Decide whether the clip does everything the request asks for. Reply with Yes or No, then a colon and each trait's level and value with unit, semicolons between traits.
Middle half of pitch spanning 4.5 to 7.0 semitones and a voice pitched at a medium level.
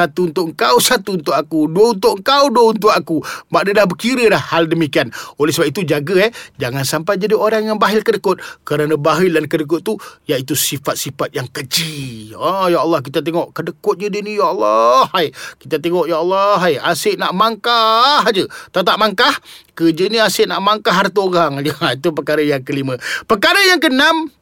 Yes: wide, 5.5 semitones; medium, 175 Hz